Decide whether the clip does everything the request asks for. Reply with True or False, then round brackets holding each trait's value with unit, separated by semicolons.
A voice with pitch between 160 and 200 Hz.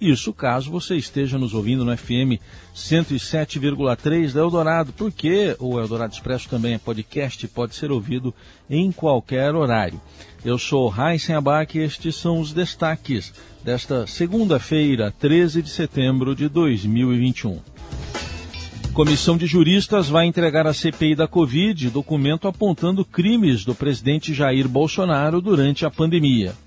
False (145 Hz)